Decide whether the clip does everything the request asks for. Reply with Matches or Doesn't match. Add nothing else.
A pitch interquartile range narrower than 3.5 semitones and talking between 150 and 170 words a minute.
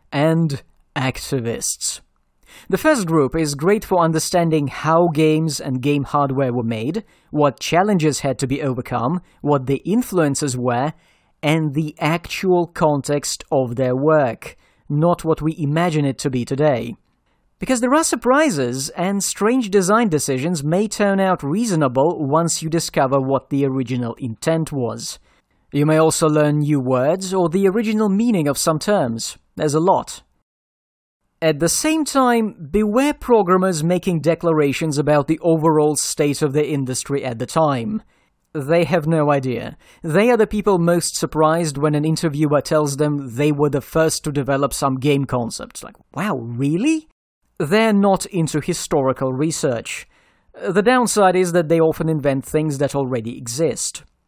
Doesn't match